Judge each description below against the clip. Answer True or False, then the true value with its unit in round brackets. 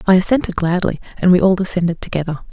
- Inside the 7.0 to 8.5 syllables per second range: True (7.1 syllables/s)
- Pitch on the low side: False (180 Hz)